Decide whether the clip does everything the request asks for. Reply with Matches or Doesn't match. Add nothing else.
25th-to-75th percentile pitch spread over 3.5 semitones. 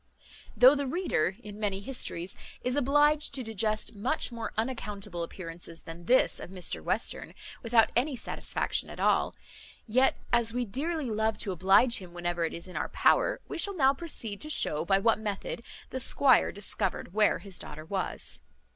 Matches